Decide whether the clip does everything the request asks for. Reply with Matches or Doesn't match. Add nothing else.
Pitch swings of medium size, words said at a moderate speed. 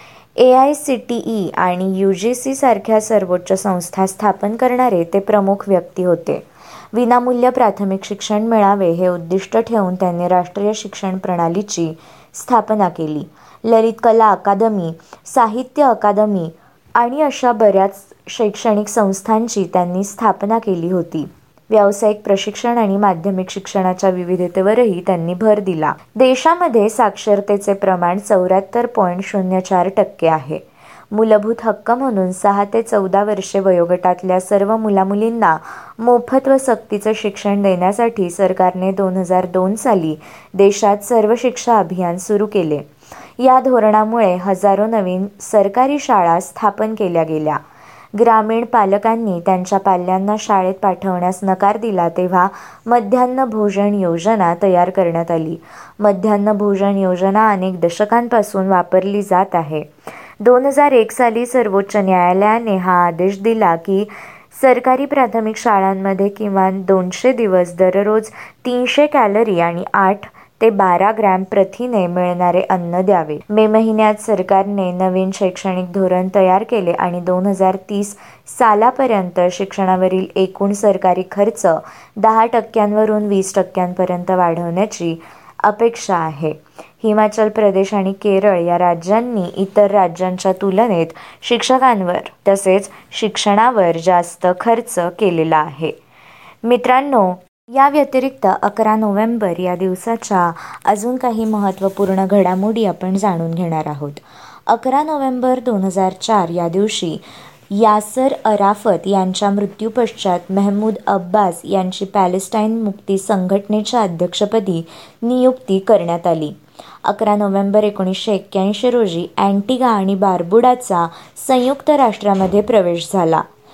Matches